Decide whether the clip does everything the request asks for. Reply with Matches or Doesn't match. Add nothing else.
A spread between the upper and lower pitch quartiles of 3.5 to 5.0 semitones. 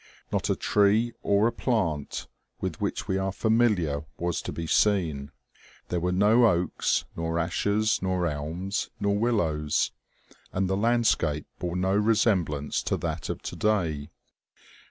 Matches